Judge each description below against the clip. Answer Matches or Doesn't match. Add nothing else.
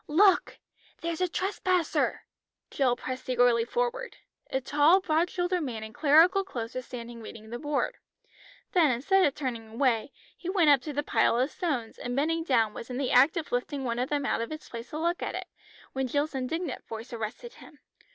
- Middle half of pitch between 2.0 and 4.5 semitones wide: Doesn't match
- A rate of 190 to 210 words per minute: Matches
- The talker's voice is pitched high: Matches